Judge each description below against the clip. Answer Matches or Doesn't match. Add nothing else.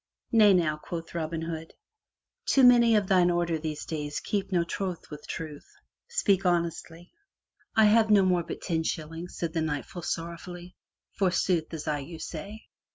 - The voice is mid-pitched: Matches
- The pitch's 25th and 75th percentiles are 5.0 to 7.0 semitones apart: Doesn't match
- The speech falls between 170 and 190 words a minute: Matches